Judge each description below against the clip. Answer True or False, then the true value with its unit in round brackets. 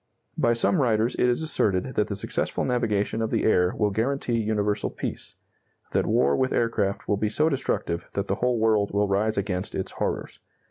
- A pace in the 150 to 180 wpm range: False (190 wpm)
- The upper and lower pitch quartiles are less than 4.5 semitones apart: True (2.9 semitones)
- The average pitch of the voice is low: True (110 Hz)